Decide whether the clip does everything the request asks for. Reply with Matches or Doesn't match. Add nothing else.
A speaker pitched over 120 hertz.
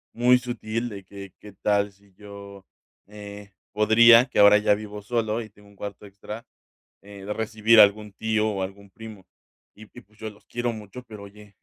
Doesn't match